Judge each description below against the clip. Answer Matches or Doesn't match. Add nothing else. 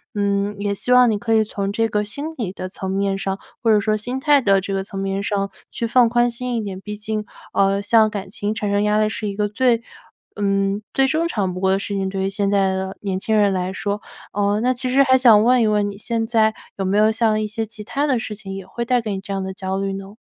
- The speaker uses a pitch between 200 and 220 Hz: Matches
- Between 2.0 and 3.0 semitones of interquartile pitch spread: Matches